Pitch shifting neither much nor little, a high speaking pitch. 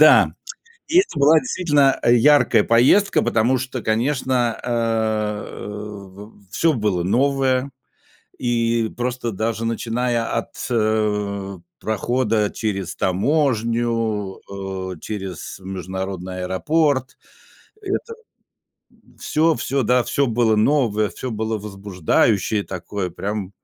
No: average, 3.9 semitones; low, 110 Hz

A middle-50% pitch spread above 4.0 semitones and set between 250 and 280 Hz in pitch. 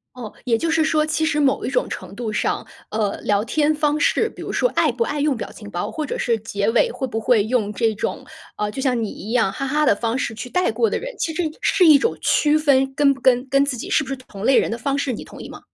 Yes: average, 5.1 semitones; very high, 260 Hz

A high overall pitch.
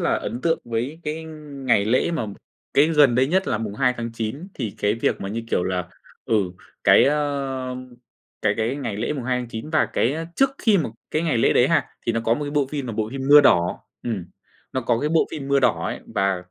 No: low, 130 Hz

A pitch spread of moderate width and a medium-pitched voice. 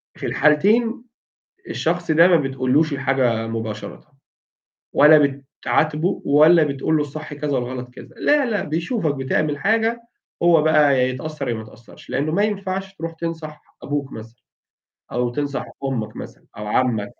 Yes: average, 4.4 semitones; medium, 150 Hz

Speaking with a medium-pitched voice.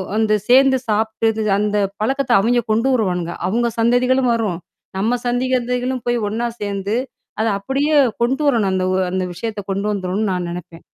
No: high, 225 Hz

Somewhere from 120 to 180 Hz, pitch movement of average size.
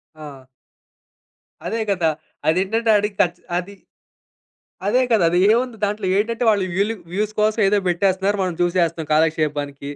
No: high, 195 Hz; average, 4.0 semitones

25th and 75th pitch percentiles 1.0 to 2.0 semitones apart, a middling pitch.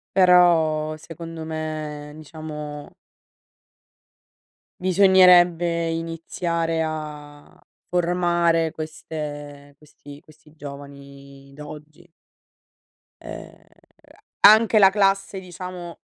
No: average, 2.8 semitones; medium, 160 Hz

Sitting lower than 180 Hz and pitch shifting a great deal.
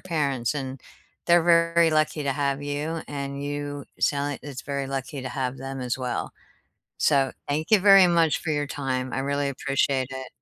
No: medium, 140 Hz; narrow, 2.4 semitones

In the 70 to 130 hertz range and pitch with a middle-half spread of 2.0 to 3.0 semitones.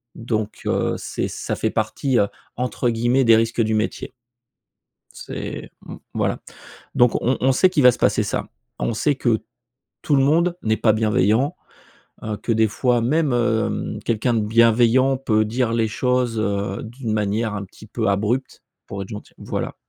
Yes: low, 115 Hz; average, 2.7 semitones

